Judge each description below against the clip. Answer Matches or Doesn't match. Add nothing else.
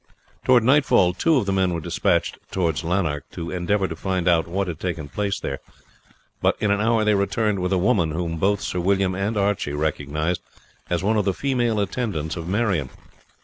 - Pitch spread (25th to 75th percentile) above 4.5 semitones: Doesn't match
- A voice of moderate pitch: Doesn't match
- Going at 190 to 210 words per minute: Matches